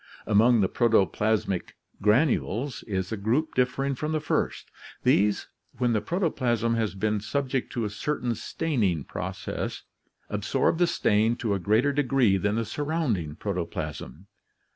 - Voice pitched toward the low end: Yes, low, 115 Hz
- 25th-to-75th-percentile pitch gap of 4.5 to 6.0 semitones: Yes, average, 5.0 semitones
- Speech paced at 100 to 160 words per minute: Yes, average, 140 wpm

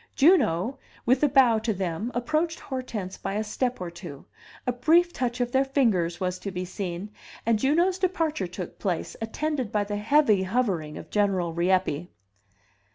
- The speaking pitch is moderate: No, high, 220 Hz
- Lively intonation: Yes, wide, 6.5 semitones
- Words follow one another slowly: No, average, 165 wpm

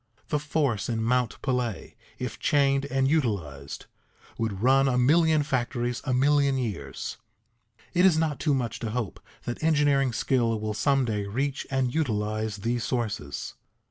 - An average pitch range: Yes, average, 4.0 semitones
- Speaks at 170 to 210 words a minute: No, average, 150 wpm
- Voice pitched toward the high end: No, low, 125 Hz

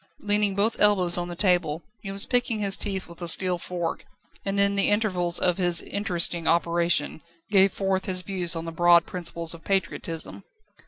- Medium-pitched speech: Yes, medium, 180 Hz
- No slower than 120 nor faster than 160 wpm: No, average, 180 wpm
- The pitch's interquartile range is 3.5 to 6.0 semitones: No, narrow, 2.6 semitones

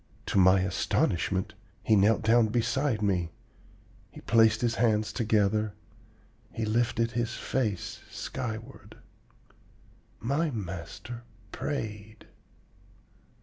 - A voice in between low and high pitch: No, low, 110 Hz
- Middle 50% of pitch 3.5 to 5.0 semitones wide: No, narrow, 2.5 semitones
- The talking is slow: Yes, slow, 95 wpm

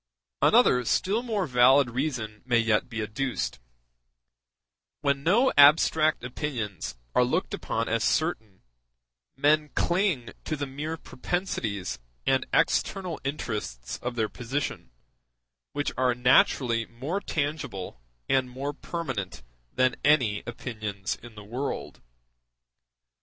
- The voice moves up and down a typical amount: Yes, average, 5.0 semitones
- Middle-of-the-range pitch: No, low, 125 Hz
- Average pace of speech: No, slow, 115 wpm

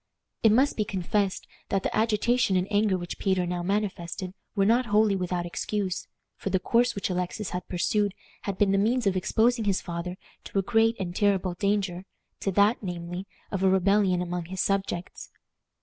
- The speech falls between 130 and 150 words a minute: No, average, 180 wpm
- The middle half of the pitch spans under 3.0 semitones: Yes, narrow, 2.6 semitones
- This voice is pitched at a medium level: No, high, 195 Hz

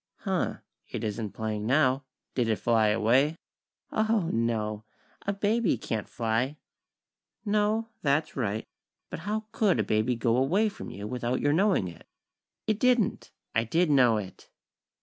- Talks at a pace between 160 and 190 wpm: No, average, 150 wpm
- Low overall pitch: Yes, low, 125 Hz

